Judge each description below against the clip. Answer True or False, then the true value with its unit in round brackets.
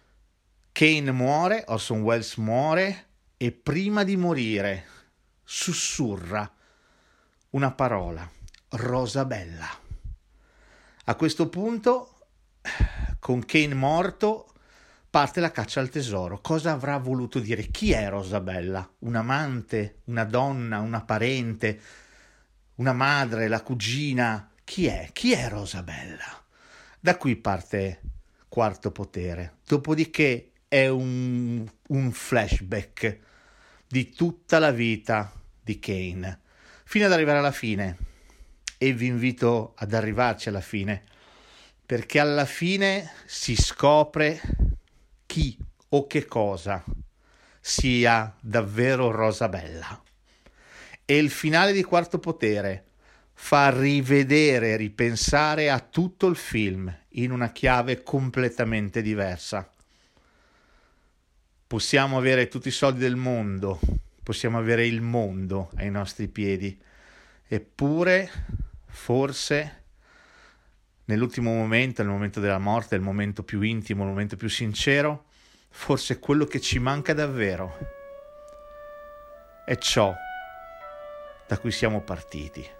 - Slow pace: True (105 wpm)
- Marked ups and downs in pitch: True (6.1 semitones)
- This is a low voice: True (120 Hz)